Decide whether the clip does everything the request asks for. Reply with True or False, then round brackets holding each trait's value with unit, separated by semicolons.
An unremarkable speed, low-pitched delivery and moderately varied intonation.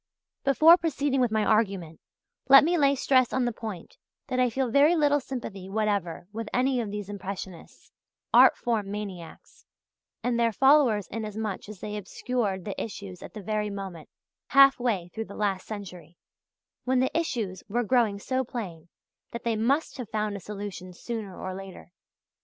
False (170 wpm; 215 Hz; 4.4 semitones)